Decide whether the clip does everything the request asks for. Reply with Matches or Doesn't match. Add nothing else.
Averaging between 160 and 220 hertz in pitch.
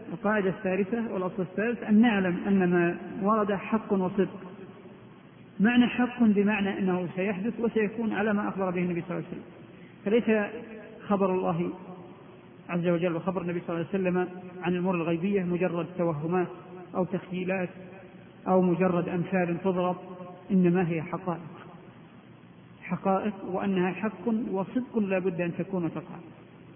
Matches